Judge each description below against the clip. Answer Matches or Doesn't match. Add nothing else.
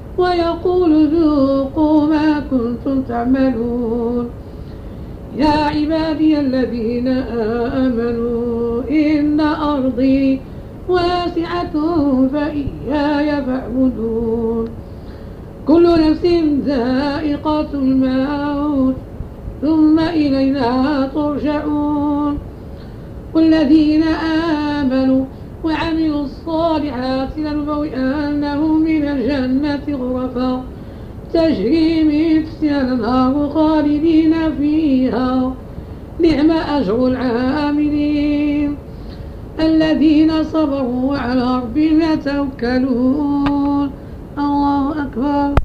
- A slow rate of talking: Matches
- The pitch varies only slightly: Doesn't match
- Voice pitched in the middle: Doesn't match